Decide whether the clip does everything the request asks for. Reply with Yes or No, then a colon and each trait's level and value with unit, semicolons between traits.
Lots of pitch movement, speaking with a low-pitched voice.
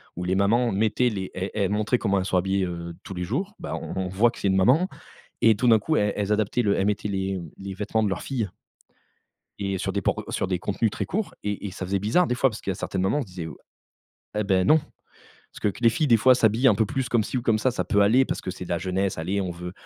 No: average, 3.4 semitones; low, 100 Hz